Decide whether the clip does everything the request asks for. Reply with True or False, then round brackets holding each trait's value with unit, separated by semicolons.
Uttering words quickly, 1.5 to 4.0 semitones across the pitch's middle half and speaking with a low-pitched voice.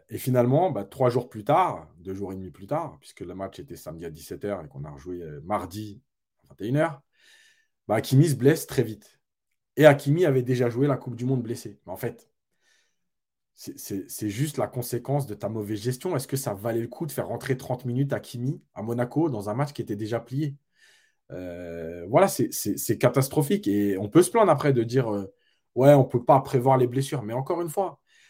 False (225 wpm; 5.2 semitones; 125 Hz)